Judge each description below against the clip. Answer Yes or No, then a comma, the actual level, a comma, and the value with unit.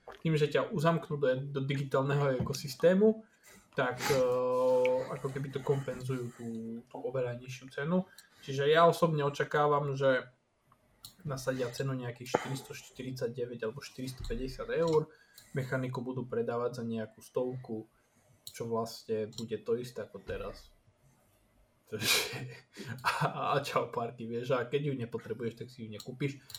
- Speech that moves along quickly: No, average, 135 wpm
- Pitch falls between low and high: No, low, 130 Hz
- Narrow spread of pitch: No, average, 3.2 semitones